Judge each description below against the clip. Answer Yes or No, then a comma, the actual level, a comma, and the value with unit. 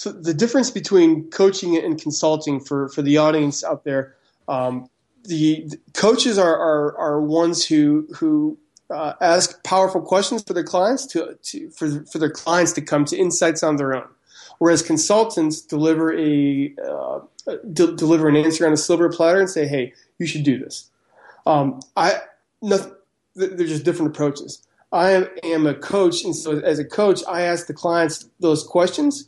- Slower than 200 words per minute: Yes, average, 175 wpm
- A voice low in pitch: No, medium, 165 Hz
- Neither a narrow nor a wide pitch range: Yes, average, 3.7 semitones